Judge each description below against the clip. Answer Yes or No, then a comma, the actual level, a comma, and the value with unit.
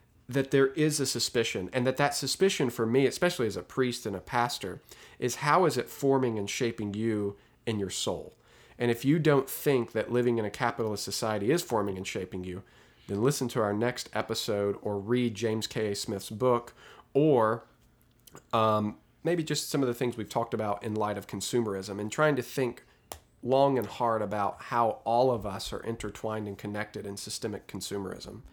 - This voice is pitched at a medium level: No, low, 115 Hz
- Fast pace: No, average, 195 wpm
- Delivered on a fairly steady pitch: No, average, 3.8 semitones